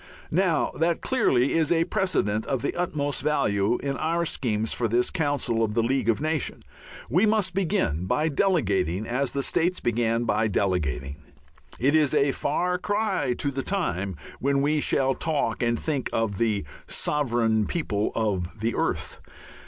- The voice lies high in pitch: No, low, 135 Hz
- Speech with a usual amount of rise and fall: No, wide, 6.5 semitones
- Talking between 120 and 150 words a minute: No, average, 160 wpm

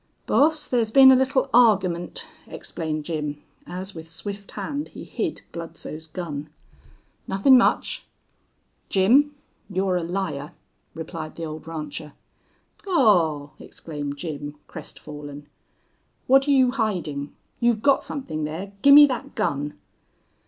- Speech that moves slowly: Yes, slow, 115 wpm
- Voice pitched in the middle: Yes, medium, 180 Hz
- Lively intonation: Yes, wide, 8.1 semitones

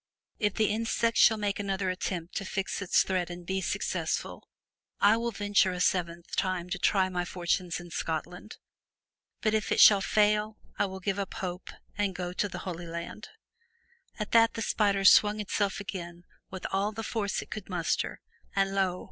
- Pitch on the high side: Yes, high, 195 Hz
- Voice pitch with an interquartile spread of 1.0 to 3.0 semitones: Yes, narrow, 2.5 semitones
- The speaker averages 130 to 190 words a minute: Yes, average, 180 wpm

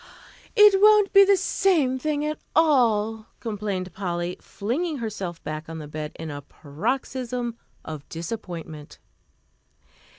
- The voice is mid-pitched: No, high, 220 Hz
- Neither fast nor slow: No, slow, 125 wpm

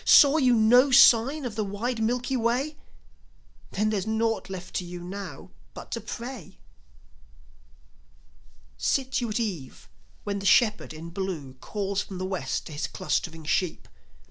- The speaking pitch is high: Yes, high, 210 Hz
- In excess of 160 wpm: No, average, 150 wpm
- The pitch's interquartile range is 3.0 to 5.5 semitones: Yes, average, 5.0 semitones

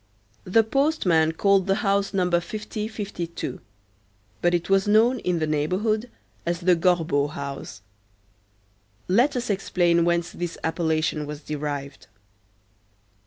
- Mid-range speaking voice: Yes, medium, 175 Hz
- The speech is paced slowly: Yes, slow, 120 wpm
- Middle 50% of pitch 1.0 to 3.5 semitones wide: No, average, 4.3 semitones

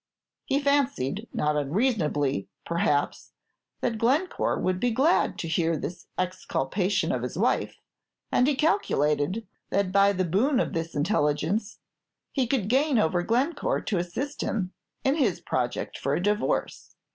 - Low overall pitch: No, high, 200 Hz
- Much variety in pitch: Yes, wide, 7.7 semitones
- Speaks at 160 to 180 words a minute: No, average, 145 wpm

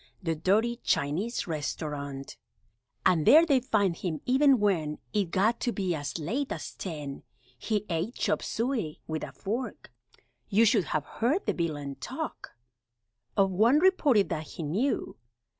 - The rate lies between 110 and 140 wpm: No, average, 150 wpm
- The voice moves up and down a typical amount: No, wide, 7.2 semitones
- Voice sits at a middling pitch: No, high, 195 Hz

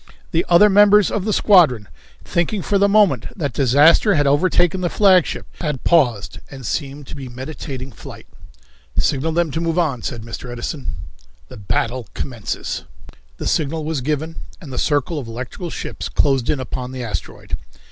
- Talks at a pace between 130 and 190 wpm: Yes, average, 165 wpm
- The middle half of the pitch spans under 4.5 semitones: No, average, 5.1 semitones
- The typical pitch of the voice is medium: Yes, medium, 150 Hz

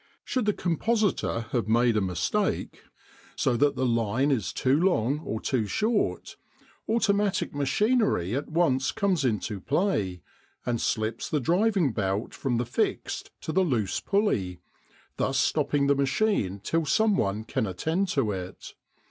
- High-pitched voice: No, low, 135 Hz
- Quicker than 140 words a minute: Yes, average, 150 wpm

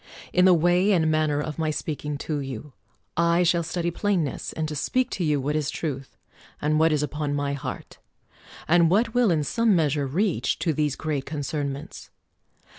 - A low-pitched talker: No, medium, 155 Hz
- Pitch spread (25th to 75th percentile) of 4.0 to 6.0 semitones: No, average, 3.0 semitones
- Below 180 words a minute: No, average, 185 wpm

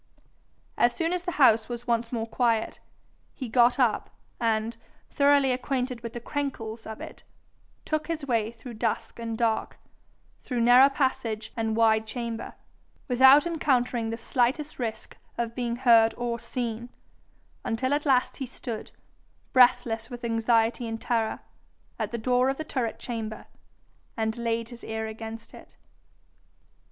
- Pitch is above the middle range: Yes, high, 235 Hz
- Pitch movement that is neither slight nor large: No, narrow, 2.3 semitones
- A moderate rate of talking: Yes, average, 145 wpm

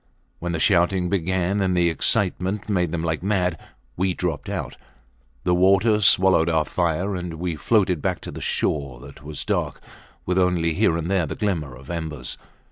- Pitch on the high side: No, very low, 90 Hz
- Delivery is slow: No, average, 180 wpm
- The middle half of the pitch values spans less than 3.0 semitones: Yes, narrow, 2.6 semitones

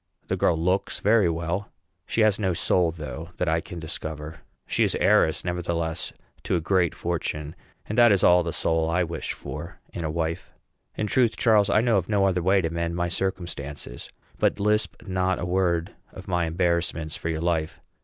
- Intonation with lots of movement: No, average, 2.7 semitones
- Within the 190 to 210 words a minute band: Yes, average, 195 wpm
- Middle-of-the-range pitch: No, very low, 85 Hz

